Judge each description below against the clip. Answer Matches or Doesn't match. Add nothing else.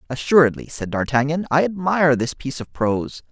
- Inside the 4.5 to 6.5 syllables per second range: Matches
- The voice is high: Doesn't match